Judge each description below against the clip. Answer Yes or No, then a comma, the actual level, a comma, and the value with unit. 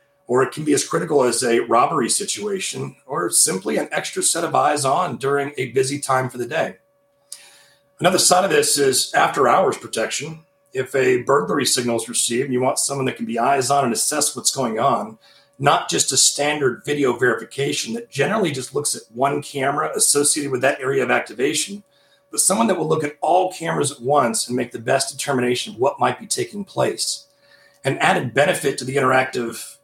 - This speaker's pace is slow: No, average, 200 wpm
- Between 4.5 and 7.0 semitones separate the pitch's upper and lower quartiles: Yes, average, 4.8 semitones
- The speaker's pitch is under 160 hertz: Yes, medium, 140 Hz